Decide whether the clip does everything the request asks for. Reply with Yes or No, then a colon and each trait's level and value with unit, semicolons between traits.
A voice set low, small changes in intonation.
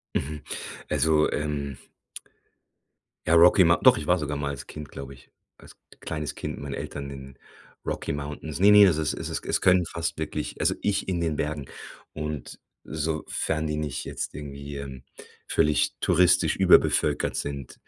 Yes: very low, 75 Hz; narrow, 2.3 semitones